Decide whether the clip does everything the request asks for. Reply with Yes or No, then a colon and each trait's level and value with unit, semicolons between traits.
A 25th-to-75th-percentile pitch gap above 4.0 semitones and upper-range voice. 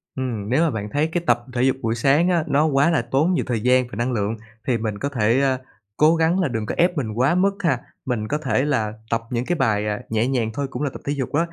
No: average, 4.7 semitones; low, 130 Hz